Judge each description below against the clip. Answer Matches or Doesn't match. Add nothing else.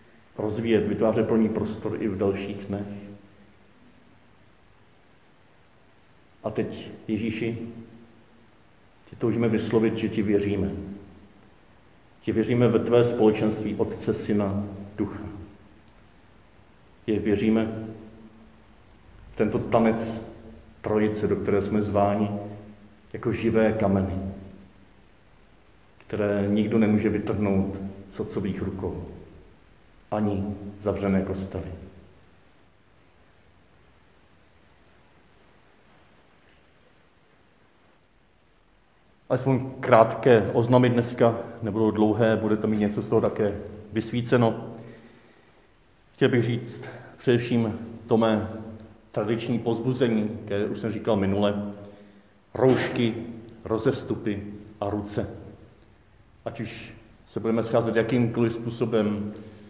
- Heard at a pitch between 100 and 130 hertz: Matches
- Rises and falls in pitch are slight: Matches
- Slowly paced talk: Matches